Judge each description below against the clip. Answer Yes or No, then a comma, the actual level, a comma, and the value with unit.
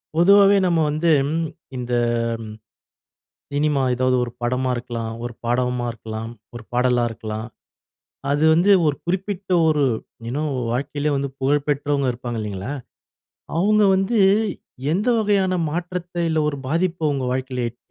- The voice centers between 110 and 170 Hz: Yes, medium, 140 Hz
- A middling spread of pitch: No, wide, 5.9 semitones